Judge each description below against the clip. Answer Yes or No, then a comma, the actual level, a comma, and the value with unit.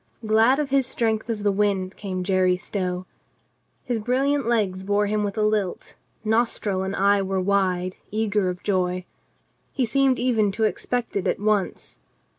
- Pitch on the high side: Yes, high, 205 Hz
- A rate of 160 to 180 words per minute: Yes, average, 165 wpm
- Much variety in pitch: No, average, 3.2 semitones